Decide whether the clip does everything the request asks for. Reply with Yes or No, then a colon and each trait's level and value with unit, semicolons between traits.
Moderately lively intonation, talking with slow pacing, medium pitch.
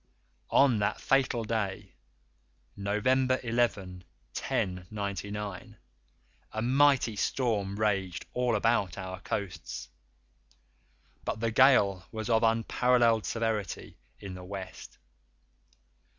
No: average, 3.3 semitones; slow, 95 wpm; low, 105 Hz